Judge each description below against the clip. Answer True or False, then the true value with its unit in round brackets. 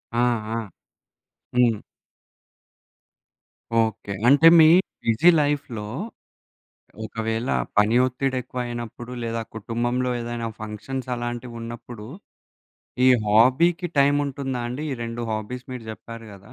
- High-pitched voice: False (120 Hz)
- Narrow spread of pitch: True (2.3 semitones)